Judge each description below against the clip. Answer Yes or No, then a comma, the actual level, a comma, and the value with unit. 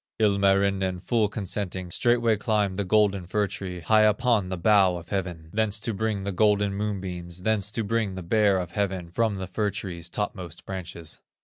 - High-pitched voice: No, low, 100 Hz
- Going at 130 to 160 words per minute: No, average, 180 wpm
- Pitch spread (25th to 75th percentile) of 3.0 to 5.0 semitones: No, narrow, 2.5 semitones